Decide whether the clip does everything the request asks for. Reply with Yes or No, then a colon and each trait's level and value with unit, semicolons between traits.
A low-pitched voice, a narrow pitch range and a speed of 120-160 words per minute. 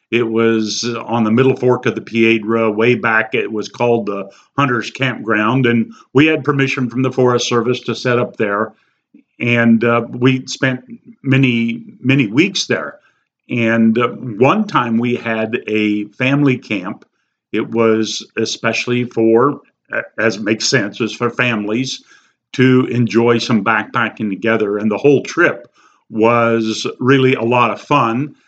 Yes: low, 120 Hz; narrow, 2.3 semitones; average, 150 wpm